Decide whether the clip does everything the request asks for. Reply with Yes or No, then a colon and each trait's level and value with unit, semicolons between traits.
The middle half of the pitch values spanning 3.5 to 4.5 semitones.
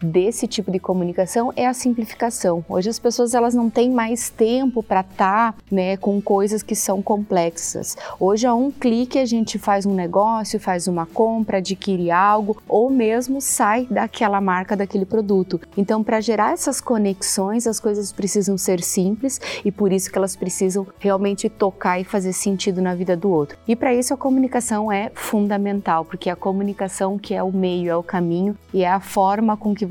No: average, 3.0 semitones